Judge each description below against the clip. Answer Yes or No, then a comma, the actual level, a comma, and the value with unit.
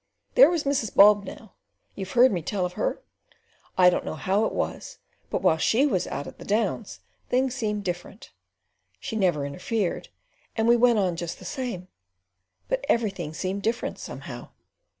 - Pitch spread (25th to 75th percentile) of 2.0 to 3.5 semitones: No, average, 4.7 semitones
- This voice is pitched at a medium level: No, high, 205 Hz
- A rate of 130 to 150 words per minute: No, average, 170 wpm